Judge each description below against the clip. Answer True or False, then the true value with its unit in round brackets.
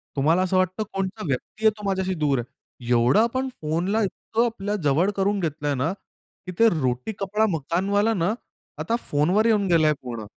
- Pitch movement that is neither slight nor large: False (5.7 semitones)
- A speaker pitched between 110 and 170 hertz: False (185 Hz)